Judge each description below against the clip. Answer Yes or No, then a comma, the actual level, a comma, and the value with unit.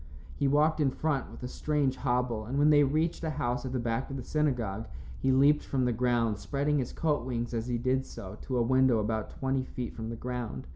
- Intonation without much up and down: No, average, 3.2 semitones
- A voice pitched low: Yes, low, 130 Hz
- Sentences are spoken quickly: Yes, fast, 235 wpm